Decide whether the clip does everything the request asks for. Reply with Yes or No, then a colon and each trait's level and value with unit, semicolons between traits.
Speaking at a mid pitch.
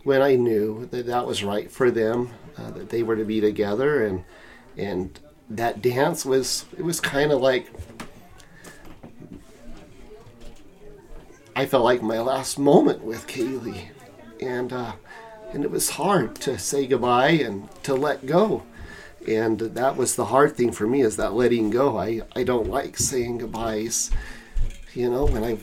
No: low, 120 Hz